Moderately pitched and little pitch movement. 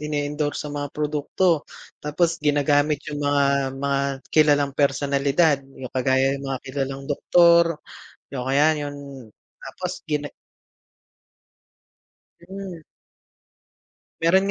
Yes: medium, 145 Hz; narrow, 1.9 semitones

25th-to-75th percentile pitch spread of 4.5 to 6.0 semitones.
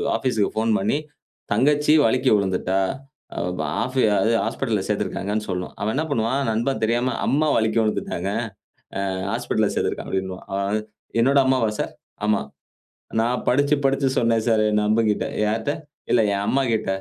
No: average, 3.6 semitones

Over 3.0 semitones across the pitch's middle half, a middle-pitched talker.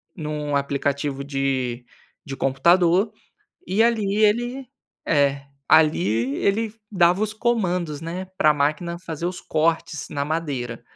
Yes: average, 5.0 semitones; medium, 160 Hz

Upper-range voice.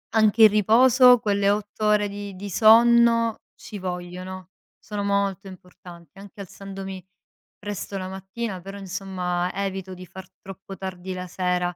Yes: high, 195 Hz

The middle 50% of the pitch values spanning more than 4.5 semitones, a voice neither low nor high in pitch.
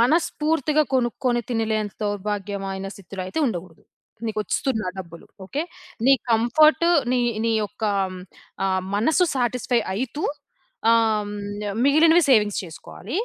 No: average, 5.1 semitones; high, 220 Hz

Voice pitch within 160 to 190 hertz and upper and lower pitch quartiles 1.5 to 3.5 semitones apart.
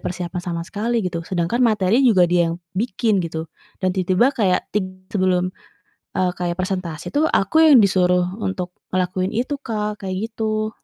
Yes: medium, 185 Hz; average, 3.2 semitones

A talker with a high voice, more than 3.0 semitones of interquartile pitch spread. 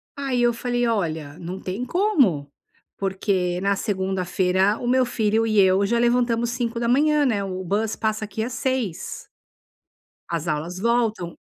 Yes: high, 215 Hz; average, 4.3 semitones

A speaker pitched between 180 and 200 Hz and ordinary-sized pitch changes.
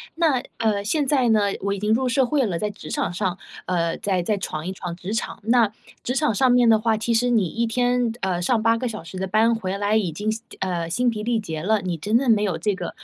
No: high, 215 Hz; average, 3.9 semitones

